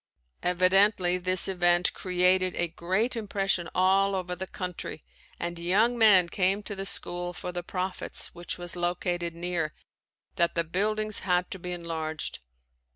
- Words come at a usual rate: Yes, average, 150 wpm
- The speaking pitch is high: No, medium, 180 Hz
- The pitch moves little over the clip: Yes, narrow, 1.8 semitones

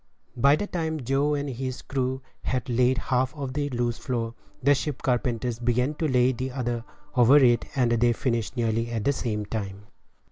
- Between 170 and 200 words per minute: Yes, average, 190 wpm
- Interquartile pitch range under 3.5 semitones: Yes, narrow, 2.5 semitones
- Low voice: Yes, low, 125 Hz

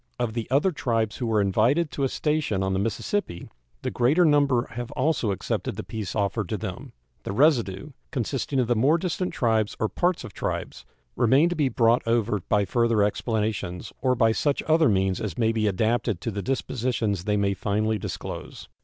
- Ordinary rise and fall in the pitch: Yes, average, 4.6 semitones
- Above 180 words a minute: Yes, average, 190 wpm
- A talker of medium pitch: No, low, 115 Hz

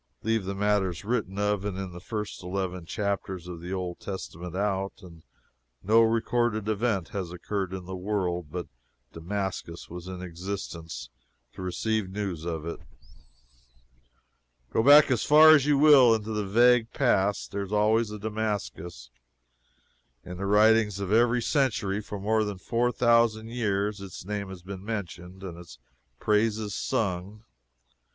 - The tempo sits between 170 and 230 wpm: No, average, 155 wpm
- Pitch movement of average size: Yes, average, 3.2 semitones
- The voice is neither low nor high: No, low, 100 Hz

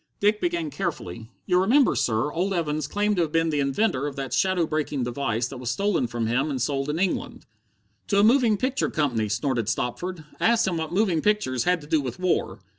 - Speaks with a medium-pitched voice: Yes, medium, 155 Hz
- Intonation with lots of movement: Yes, wide, 7.1 semitones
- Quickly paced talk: Yes, fast, 215 wpm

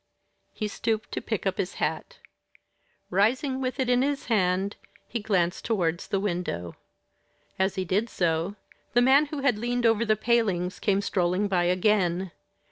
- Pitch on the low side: No, high, 205 Hz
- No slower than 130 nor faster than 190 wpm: Yes, average, 160 wpm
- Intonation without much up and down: No, average, 4.6 semitones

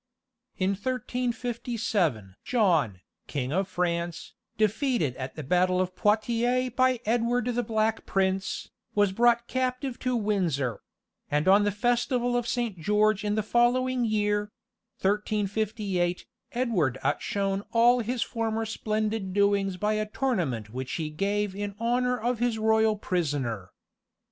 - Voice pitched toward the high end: Yes, high, 210 Hz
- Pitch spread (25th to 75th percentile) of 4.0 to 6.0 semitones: Yes, average, 4.3 semitones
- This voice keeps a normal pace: No, slow, 130 wpm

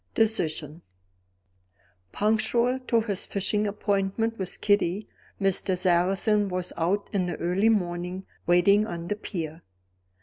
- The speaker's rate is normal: No, slow, 115 wpm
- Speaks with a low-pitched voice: No, high, 195 Hz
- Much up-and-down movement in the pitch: No, average, 3.1 semitones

